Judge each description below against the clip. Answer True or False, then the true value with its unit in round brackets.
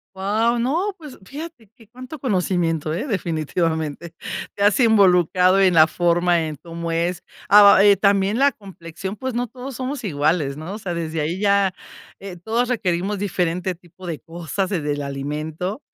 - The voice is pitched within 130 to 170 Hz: False (185 Hz)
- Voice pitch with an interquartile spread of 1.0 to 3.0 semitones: False (4.5 semitones)